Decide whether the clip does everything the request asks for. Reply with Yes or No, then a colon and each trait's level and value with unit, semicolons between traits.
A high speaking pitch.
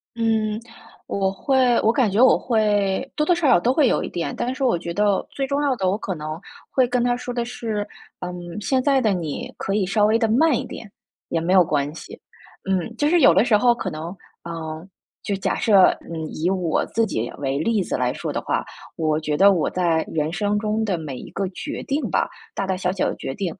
Yes: high, 200 Hz